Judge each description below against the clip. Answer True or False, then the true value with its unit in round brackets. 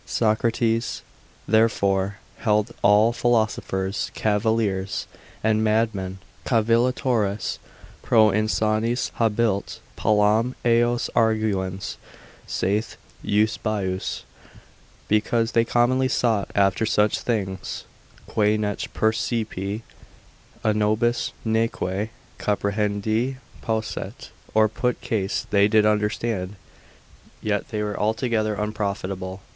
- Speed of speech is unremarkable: False (95 wpm)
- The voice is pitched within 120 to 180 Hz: False (110 Hz)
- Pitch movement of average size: False (1.9 semitones)